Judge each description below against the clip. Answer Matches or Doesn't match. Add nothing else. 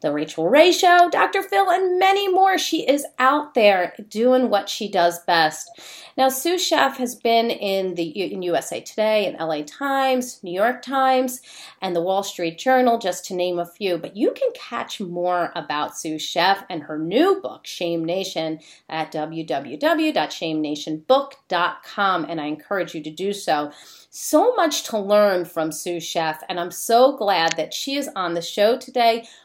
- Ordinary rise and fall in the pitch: Doesn't match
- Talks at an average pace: Matches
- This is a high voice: Matches